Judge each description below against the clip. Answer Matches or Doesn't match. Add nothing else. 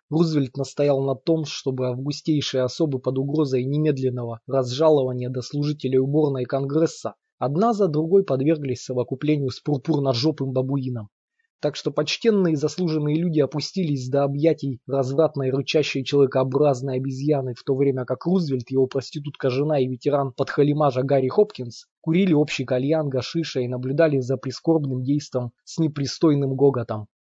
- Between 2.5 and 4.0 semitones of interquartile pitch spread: Matches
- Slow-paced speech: Doesn't match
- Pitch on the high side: Doesn't match